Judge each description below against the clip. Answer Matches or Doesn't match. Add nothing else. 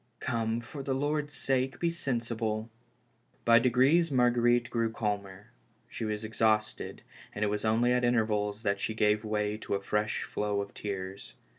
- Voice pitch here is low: Matches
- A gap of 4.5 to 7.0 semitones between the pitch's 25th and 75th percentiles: Doesn't match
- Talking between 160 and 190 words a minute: Matches